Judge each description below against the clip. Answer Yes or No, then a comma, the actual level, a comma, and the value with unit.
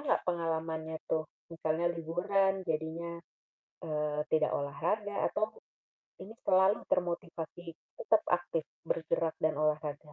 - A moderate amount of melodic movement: No, narrow, 2.3 semitones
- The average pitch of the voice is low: No, medium, 165 Hz